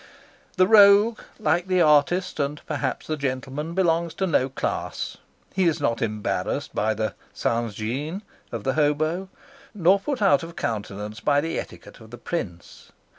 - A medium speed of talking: Yes, average, 150 wpm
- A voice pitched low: No, medium, 150 Hz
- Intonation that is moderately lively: No, wide, 7.2 semitones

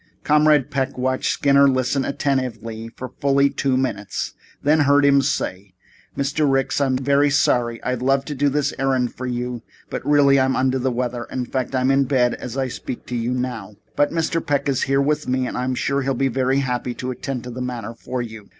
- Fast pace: Yes, fast, 210 wpm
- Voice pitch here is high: No, low, 130 Hz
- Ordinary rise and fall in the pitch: No, narrow, 1.9 semitones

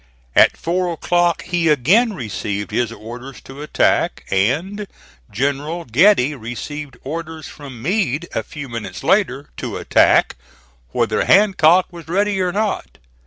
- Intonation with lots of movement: Yes, wide, 6.2 semitones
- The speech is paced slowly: Yes, slow, 130 wpm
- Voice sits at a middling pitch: Yes, medium, 150 Hz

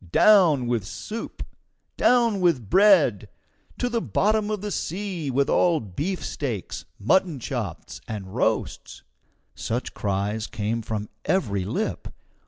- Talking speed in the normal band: No, slow, 120 wpm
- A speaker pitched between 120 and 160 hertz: Yes, medium, 140 Hz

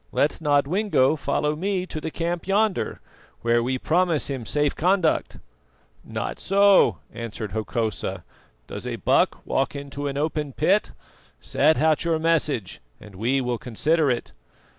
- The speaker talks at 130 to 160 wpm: Yes, average, 140 wpm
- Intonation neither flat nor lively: Yes, average, 5.0 semitones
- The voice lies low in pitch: No, medium, 145 Hz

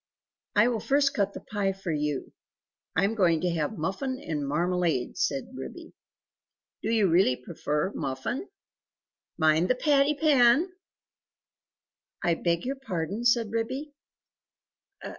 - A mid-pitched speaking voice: No, high, 195 Hz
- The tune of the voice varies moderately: No, wide, 7.7 semitones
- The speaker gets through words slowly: Yes, slow, 130 wpm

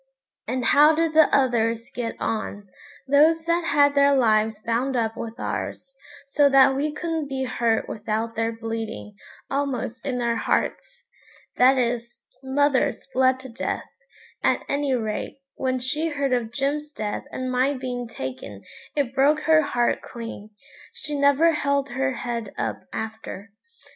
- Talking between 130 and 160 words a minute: Yes, average, 150 wpm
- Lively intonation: No, average, 3.7 semitones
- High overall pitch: Yes, very high, 260 Hz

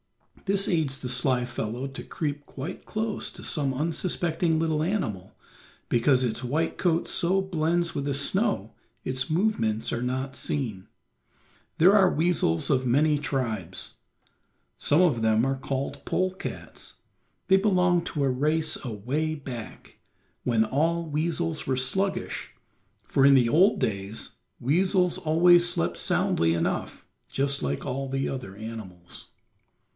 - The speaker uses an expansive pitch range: Yes, wide, 5.7 semitones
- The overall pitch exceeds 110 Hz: Yes, medium, 140 Hz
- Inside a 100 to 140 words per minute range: Yes, slow, 135 wpm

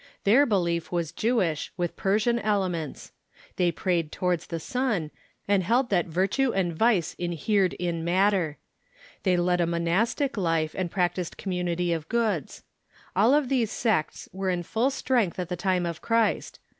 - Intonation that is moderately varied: Yes, average, 4.3 semitones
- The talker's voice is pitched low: No, medium, 180 Hz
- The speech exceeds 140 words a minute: Yes, average, 160 wpm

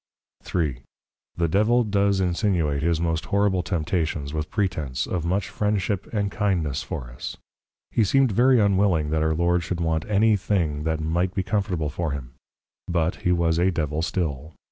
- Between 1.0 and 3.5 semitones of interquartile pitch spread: No, average, 4.1 semitones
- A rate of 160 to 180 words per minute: Yes, average, 170 wpm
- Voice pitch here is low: Yes, very low, 85 Hz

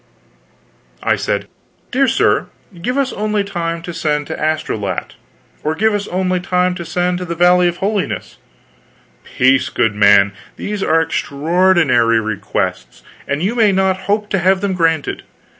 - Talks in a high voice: No, medium, 175 Hz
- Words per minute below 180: Yes, average, 160 wpm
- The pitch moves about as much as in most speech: Yes, average, 4.1 semitones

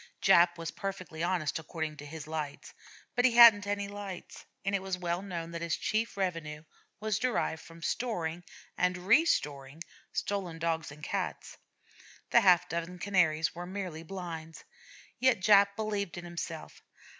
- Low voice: No, medium, 180 Hz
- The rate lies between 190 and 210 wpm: No, average, 155 wpm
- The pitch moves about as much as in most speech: Yes, average, 3.6 semitones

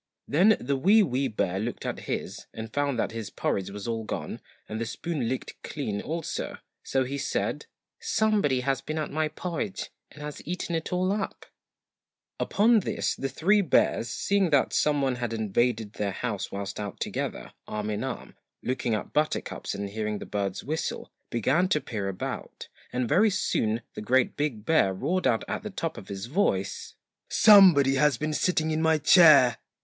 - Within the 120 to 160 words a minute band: No, average, 175 wpm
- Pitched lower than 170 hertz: Yes, low, 135 Hz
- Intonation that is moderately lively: No, wide, 6.7 semitones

